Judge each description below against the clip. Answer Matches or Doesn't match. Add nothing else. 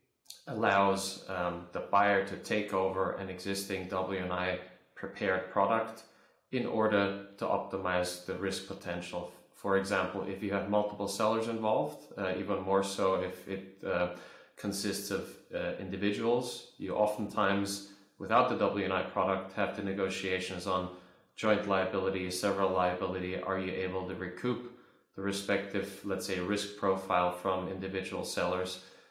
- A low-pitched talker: Matches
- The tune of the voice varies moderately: Doesn't match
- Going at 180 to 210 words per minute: Doesn't match